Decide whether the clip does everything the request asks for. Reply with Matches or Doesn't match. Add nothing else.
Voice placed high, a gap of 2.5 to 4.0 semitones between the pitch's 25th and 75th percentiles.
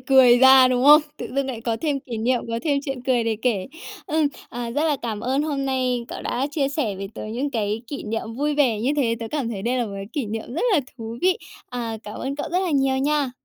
Matches